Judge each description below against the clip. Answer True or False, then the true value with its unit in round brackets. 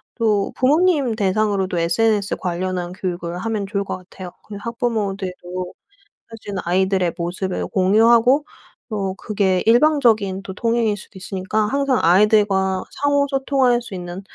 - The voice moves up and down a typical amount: True (3.7 semitones)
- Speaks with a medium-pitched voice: False (200 Hz)